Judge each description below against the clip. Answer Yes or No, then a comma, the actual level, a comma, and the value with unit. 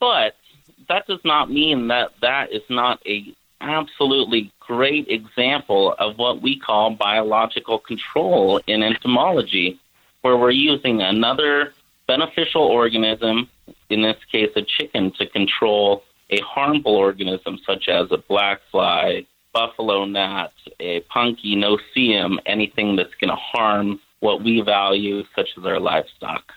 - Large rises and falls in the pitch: No, average, 4.3 semitones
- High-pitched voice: No, low, 110 Hz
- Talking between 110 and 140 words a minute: Yes, slow, 135 wpm